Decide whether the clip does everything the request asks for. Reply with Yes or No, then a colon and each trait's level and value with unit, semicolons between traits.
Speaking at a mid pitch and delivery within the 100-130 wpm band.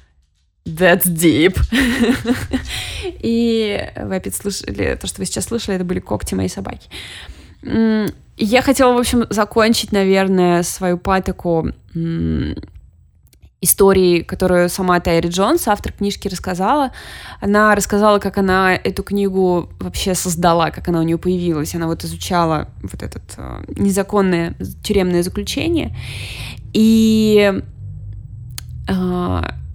Yes: medium, 180 Hz; slow, 110 wpm